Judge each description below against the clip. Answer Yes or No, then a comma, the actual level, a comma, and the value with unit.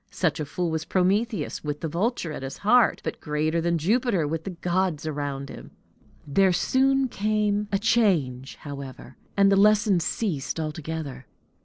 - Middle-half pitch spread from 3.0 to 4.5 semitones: No, wide, 5.5 semitones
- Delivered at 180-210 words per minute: No, average, 160 wpm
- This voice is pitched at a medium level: Yes, medium, 170 Hz